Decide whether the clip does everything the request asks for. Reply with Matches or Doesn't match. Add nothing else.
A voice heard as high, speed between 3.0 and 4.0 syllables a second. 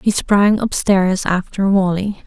Matches